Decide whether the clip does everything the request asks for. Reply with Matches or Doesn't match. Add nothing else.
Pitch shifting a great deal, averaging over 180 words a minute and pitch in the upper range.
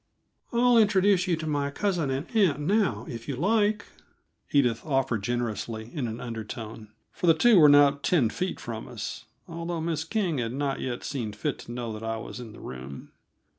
Doesn't match